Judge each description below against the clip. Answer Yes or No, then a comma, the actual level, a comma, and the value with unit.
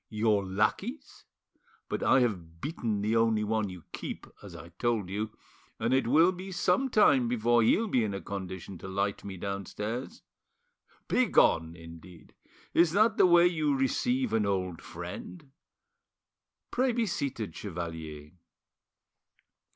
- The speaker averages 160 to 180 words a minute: No, average, 140 wpm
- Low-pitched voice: Yes, low, 110 Hz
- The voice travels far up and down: Yes, wide, 7.4 semitones